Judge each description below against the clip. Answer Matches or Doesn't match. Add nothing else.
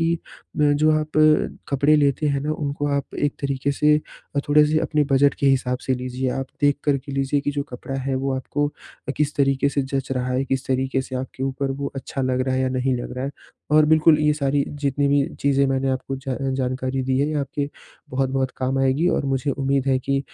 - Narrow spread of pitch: Matches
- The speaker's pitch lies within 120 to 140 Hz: Matches